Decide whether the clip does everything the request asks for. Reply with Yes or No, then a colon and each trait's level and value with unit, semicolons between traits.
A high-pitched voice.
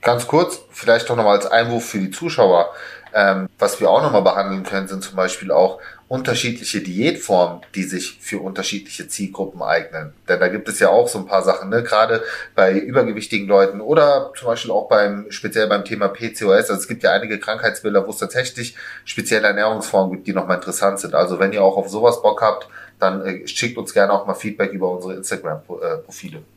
No: low, 100 Hz